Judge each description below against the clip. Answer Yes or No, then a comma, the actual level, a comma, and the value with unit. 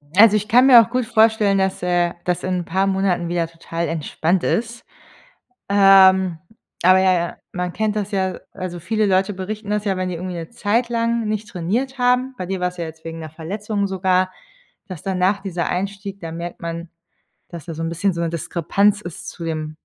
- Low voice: No, high, 190 Hz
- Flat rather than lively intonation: No, average, 3.3 semitones